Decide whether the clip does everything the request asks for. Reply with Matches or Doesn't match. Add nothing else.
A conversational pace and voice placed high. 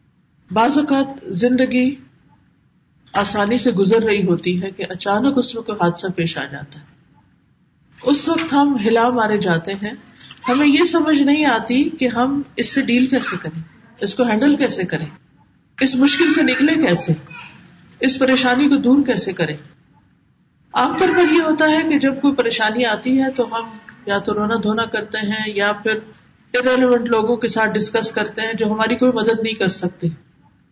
Matches